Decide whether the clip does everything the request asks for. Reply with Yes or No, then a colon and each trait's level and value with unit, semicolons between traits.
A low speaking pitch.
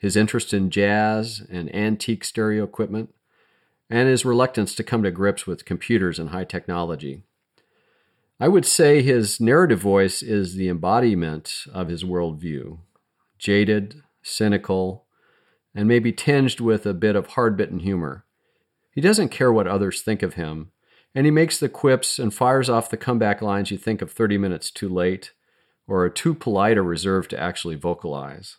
Yes: low, 100 Hz